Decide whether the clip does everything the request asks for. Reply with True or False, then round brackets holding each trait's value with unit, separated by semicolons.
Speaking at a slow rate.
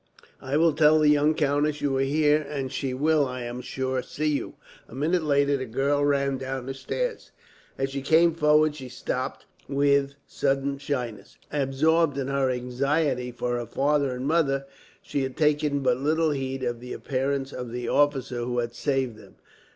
False (180 wpm)